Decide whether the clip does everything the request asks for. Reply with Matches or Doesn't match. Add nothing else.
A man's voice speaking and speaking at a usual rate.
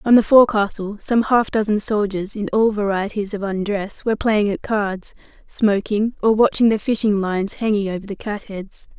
Doesn't match